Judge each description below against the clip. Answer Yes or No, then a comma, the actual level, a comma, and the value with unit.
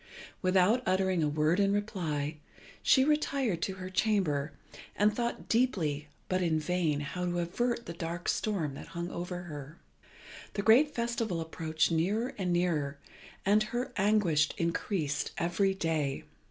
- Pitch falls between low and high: Yes, medium, 180 Hz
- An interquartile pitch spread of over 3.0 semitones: Yes, average, 4.7 semitones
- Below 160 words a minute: Yes, average, 145 wpm